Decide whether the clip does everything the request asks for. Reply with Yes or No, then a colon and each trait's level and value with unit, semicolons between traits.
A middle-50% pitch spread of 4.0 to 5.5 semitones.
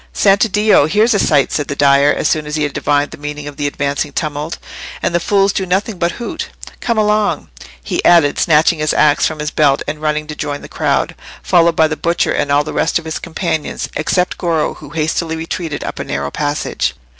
No: average, 2.9 semitones